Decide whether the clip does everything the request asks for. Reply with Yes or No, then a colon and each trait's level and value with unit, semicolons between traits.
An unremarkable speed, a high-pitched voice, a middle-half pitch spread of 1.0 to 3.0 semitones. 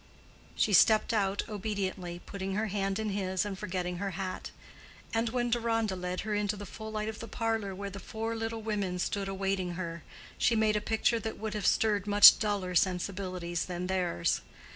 Yes: average, 185 wpm; high, 200 Hz; average, 2.7 semitones